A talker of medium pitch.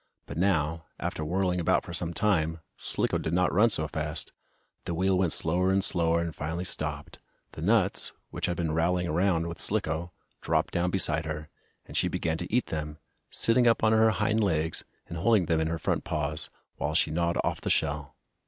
No: very low, 85 Hz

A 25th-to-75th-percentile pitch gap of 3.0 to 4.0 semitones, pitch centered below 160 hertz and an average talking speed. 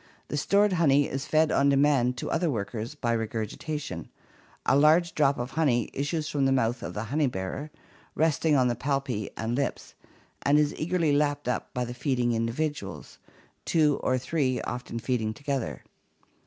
Yes: average, 3.7 semitones; medium, 140 Hz; average, 170 wpm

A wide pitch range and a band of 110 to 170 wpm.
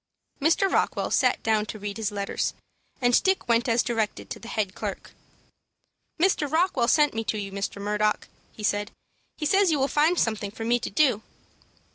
No: wide, 6.1 semitones; average, 185 wpm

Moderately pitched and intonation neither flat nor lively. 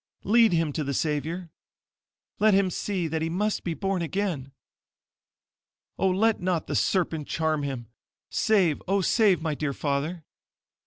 Yes: medium, 170 Hz; average, 4.1 semitones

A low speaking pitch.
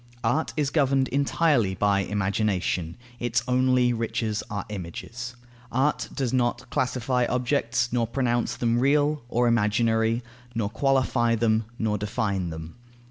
Yes: low, 120 Hz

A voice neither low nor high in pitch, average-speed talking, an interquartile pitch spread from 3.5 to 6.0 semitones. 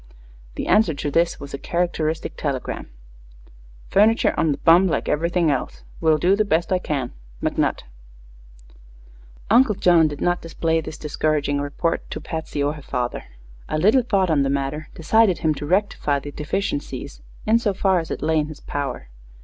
Yes: medium, 160 Hz; average, 175 wpm; average, 3.9 semitones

